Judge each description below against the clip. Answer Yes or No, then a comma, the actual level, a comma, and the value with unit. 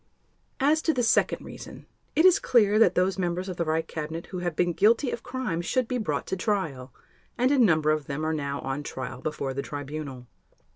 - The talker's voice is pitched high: No, medium, 175 Hz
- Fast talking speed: Yes, fast, 210 wpm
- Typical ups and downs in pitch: No, wide, 7.0 semitones